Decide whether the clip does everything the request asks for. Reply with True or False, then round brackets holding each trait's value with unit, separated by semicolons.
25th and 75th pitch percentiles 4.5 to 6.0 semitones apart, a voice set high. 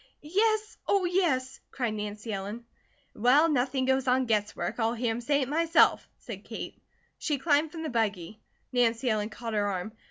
True (5.3 semitones; 250 Hz)